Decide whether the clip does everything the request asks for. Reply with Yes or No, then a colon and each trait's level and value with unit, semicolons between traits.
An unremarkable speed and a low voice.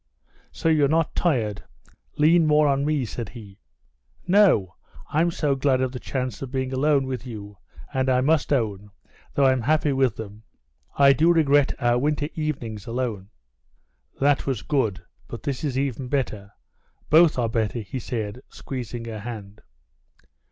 Yes: average, 160 wpm; low, 130 Hz